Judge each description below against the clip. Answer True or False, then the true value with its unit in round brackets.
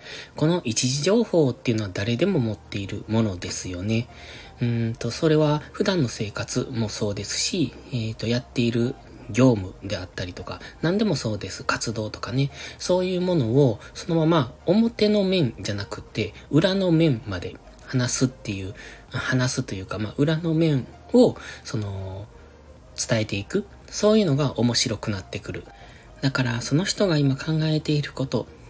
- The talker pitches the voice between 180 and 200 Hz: False (125 Hz)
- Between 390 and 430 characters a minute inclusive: False (315 characters per minute)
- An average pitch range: False (6.3 semitones)